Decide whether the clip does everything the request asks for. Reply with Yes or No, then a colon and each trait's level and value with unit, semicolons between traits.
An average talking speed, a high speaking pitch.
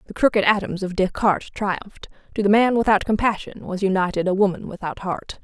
Yes: average, 190 wpm; high, 200 Hz